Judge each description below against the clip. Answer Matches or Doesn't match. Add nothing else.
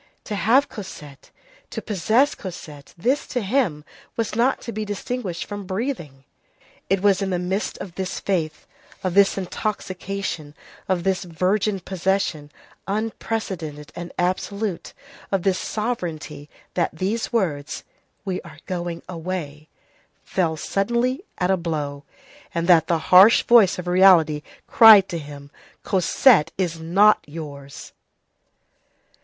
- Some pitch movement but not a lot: Matches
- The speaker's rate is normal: Doesn't match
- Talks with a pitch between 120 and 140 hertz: Doesn't match